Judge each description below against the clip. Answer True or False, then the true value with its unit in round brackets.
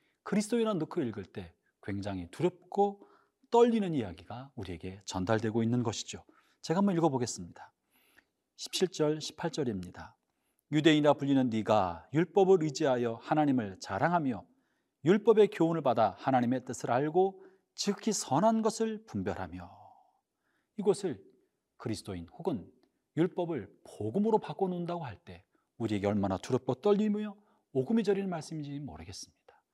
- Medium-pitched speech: True (150 Hz)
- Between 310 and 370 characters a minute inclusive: True (315 characters per minute)